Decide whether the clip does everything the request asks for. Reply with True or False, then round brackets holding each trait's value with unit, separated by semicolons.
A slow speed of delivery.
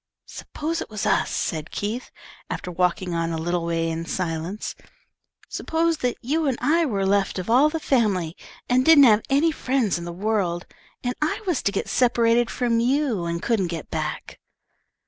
False (180 wpm)